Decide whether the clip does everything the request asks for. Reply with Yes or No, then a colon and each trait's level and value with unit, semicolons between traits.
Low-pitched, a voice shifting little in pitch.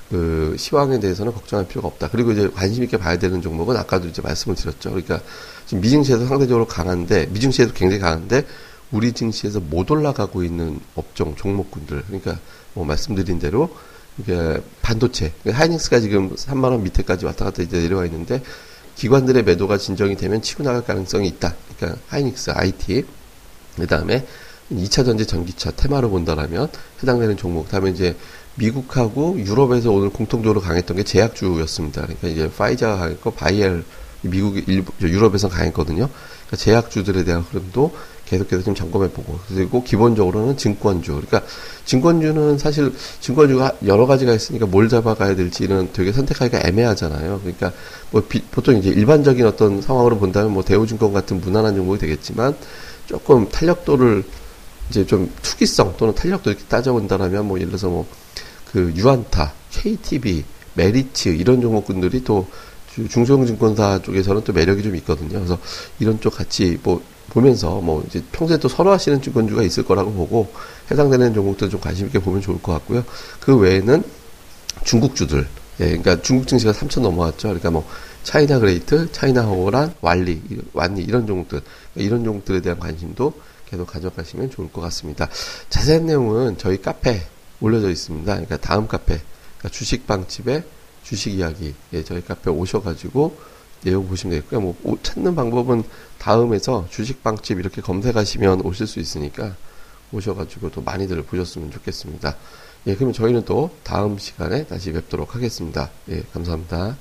No: low, 100 Hz; average, 5.2 semitones